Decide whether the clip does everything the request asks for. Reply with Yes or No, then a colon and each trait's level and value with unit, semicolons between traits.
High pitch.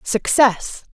Yes: high, 245 Hz